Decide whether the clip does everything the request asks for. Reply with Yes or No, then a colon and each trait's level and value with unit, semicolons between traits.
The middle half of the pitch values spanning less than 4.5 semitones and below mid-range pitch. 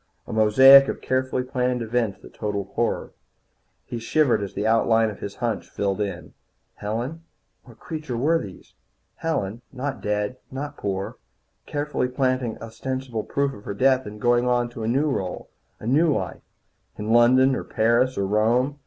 Yes: average, 3.7 semitones; low, 120 Hz